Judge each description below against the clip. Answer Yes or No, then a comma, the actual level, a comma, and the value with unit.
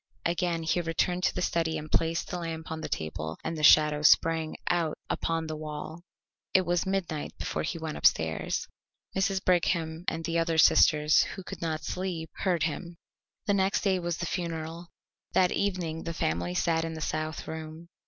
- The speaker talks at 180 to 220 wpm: Yes, average, 185 wpm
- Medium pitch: Yes, medium, 165 Hz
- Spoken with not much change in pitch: Yes, narrow, 1.8 semitones